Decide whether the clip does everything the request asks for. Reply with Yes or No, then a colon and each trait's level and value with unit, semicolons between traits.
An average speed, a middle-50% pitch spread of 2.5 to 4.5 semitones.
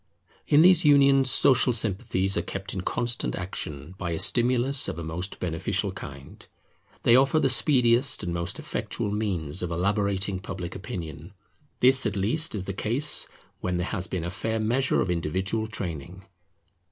No: average, 165 wpm; wide, 5.4 semitones